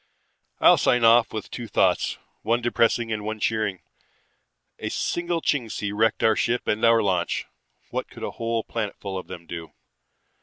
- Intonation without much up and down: Yes, narrow, 2.1 semitones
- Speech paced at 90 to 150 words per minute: No, average, 160 wpm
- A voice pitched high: No, low, 110 Hz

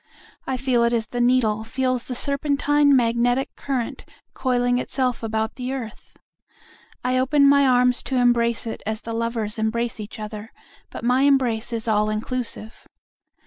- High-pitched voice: Yes, high, 245 Hz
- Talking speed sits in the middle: Yes, average, 150 wpm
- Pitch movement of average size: No, narrow, 2.3 semitones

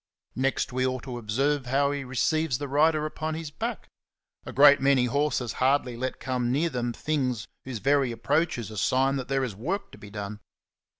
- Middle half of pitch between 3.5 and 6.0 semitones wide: No, average, 2.8 semitones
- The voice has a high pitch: No, low, 135 Hz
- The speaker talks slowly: No, average, 195 wpm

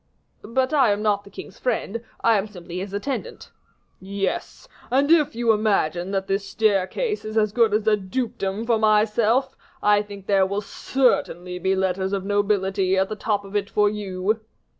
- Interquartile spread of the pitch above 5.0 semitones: No, narrow, 2.6 semitones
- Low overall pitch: No, high, 205 Hz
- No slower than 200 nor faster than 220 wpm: No, average, 180 wpm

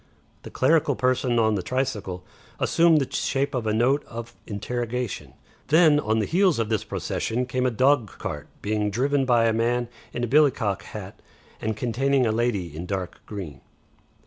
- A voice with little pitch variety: No, average, 3.7 semitones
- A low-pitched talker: Yes, low, 120 Hz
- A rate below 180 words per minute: Yes, average, 165 wpm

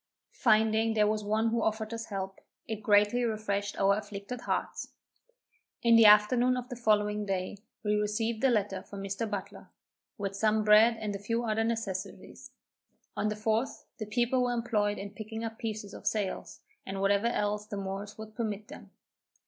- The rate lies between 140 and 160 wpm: No, average, 175 wpm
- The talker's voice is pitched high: Yes, high, 215 Hz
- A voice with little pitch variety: Yes, narrow, 1.8 semitones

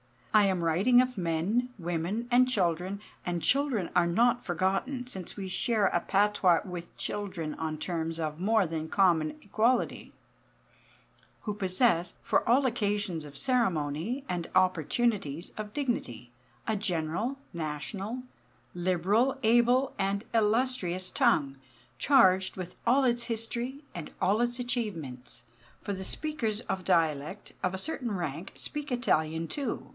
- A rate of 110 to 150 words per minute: Yes, slow, 135 wpm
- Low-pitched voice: No, high, 195 Hz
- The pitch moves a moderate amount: No, wide, 5.9 semitones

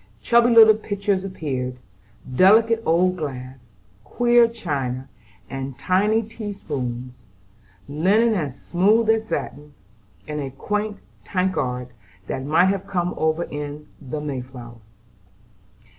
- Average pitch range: No, wide, 7.5 semitones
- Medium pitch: Yes, medium, 170 Hz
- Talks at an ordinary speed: No, slow, 115 wpm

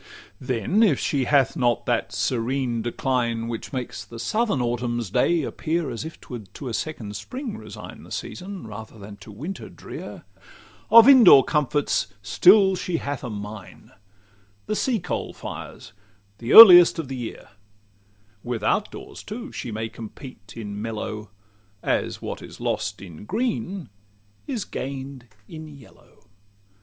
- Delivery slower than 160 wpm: Yes, average, 150 wpm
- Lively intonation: Yes, wide, 7.7 semitones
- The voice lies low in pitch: Yes, low, 130 Hz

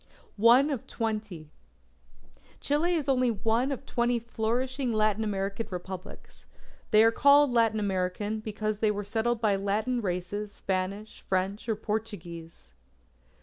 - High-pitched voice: Yes, high, 215 Hz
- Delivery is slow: Yes, slow, 130 wpm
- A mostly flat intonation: No, average, 3.3 semitones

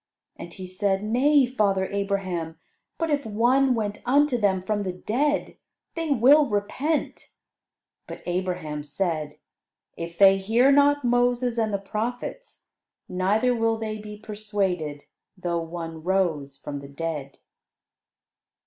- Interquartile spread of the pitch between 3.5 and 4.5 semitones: No, wide, 5.5 semitones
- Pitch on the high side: Yes, high, 205 Hz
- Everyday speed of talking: No, slow, 130 wpm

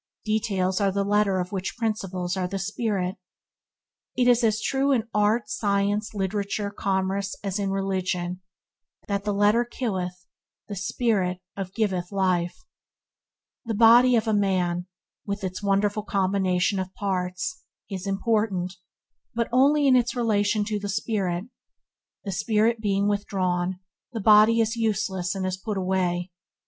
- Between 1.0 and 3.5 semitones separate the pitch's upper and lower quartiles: Yes, narrow, 2.5 semitones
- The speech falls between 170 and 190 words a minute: No, average, 145 wpm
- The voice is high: Yes, high, 200 Hz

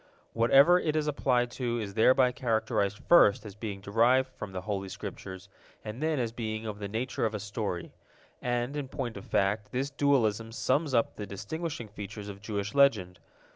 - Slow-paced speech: No, average, 180 wpm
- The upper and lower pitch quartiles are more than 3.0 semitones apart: Yes, average, 4.1 semitones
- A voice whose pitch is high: No, low, 115 Hz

